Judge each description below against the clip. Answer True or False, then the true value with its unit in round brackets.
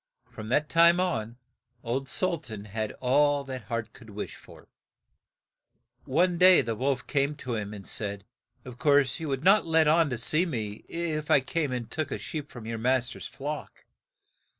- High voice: False (135 Hz)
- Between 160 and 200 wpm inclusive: True (190 wpm)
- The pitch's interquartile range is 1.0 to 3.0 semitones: False (5.1 semitones)